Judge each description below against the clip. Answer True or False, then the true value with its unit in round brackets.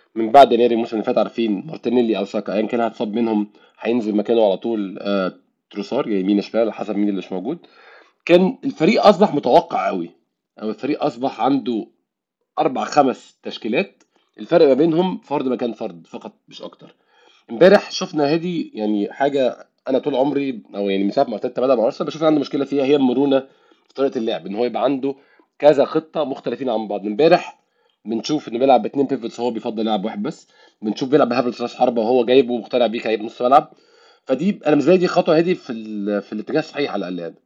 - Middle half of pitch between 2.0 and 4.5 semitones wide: False (5.1 semitones)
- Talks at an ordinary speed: False (190 wpm)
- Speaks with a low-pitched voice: True (120 Hz)